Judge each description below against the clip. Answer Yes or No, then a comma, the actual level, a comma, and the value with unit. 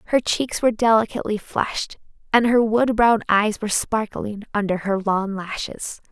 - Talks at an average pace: Yes, average, 155 wpm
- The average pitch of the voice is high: Yes, high, 215 Hz